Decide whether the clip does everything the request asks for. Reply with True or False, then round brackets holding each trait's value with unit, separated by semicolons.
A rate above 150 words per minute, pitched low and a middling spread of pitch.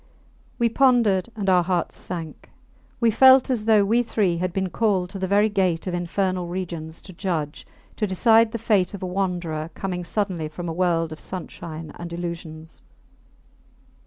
False (170 wpm; 185 Hz; 3.5 semitones)